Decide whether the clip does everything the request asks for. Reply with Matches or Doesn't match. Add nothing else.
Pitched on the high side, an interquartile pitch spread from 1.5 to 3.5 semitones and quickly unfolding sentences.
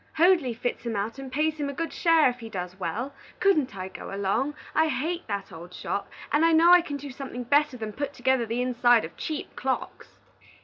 Doesn't match